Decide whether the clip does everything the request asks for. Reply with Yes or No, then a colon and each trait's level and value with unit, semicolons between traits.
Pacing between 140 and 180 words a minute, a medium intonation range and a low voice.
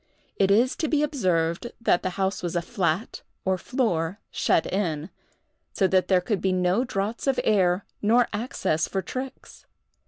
No: average, 165 wpm; average, 4.7 semitones; high, 195 Hz